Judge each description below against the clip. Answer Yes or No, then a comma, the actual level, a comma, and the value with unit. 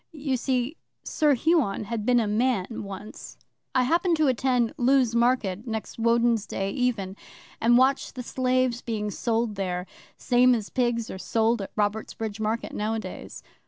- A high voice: Yes, high, 235 Hz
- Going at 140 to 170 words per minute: Yes, average, 155 wpm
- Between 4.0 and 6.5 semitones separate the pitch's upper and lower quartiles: No, average, 3.0 semitones